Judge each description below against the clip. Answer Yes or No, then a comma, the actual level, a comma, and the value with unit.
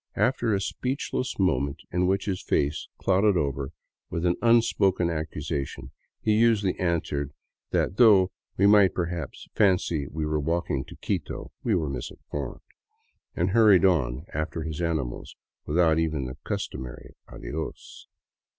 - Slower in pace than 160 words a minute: Yes, average, 140 wpm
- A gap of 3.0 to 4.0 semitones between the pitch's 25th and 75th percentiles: No, average, 4.9 semitones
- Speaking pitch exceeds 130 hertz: No, very low, 85 Hz